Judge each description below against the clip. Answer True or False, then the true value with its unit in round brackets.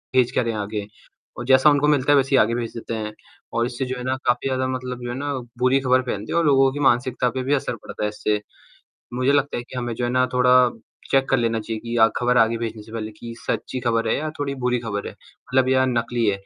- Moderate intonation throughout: False (2.2 semitones)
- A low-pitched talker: True (125 Hz)